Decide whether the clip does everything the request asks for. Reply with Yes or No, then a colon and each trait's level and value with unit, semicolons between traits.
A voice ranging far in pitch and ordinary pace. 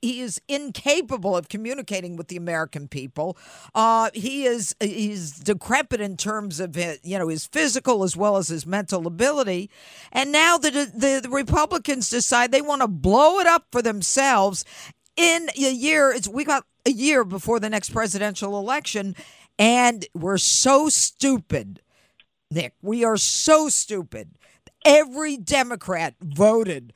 Yes: wide, 6.1 semitones; average, 155 wpm